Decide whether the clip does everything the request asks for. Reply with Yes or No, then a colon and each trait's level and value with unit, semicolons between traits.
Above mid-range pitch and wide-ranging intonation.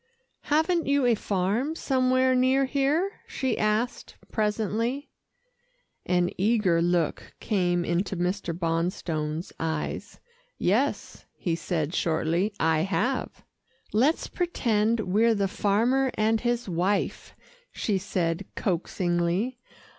Yes: high, 205 Hz; wide, 6.2 semitones